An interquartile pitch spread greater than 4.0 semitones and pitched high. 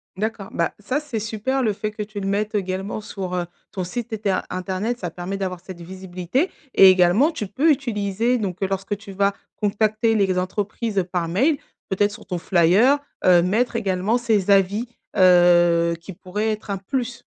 No: average, 3.1 semitones; high, 200 Hz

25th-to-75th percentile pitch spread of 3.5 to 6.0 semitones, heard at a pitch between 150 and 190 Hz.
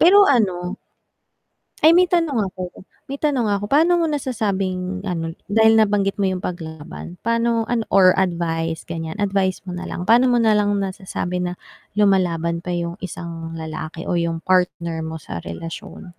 Yes: average, 4.6 semitones; medium, 185 Hz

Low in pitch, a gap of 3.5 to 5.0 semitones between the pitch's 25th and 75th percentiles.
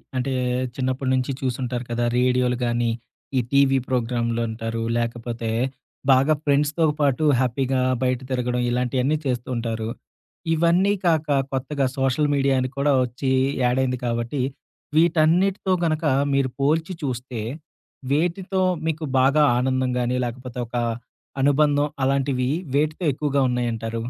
No: low, 130 Hz; average, 2.9 semitones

